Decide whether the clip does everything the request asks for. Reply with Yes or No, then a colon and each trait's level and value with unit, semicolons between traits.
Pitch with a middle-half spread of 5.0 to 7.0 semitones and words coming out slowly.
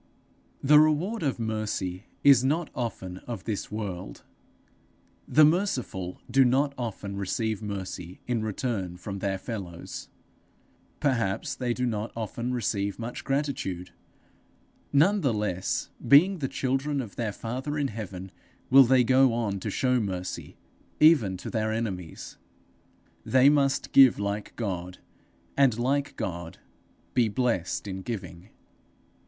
Yes: wide, 5.5 semitones; slow, 130 wpm